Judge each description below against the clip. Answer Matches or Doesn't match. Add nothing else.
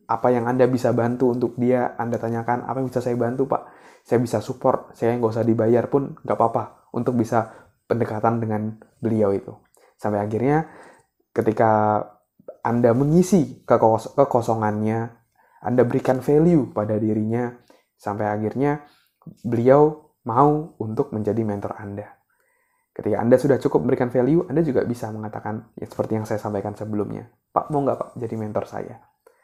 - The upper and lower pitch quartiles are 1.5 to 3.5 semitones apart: Matches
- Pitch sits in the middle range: Doesn't match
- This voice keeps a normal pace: Doesn't match